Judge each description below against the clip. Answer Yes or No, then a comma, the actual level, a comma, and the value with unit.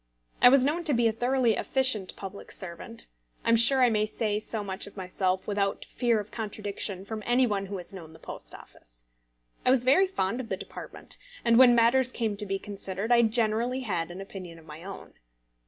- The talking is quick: Yes, fast, 210 wpm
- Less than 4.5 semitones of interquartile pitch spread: Yes, average, 3.9 semitones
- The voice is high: Yes, high, 215 Hz